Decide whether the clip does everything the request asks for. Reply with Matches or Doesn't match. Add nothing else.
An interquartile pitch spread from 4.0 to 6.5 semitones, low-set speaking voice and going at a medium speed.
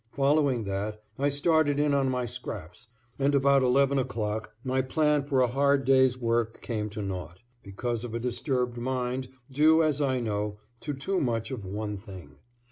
Matches